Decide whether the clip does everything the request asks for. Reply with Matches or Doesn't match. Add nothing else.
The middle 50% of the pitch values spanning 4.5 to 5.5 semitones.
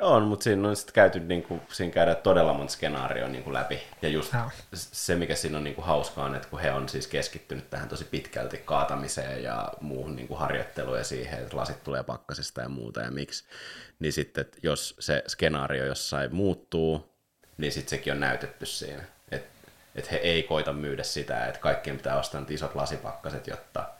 Matches